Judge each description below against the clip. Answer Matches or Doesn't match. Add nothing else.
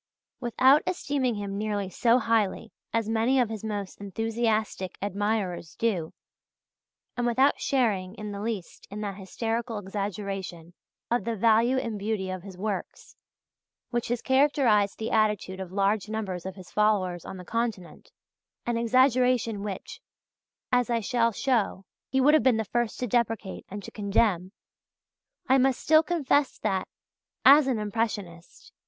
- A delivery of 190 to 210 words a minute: Doesn't match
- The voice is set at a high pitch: Matches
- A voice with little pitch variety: Doesn't match